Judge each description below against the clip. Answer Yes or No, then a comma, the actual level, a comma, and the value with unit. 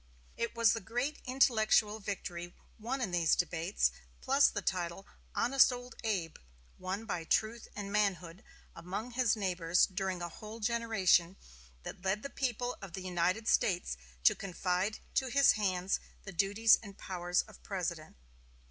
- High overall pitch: Yes, high, 200 Hz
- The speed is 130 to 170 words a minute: Yes, average, 150 wpm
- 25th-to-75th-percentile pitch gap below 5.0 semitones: Yes, average, 4.2 semitones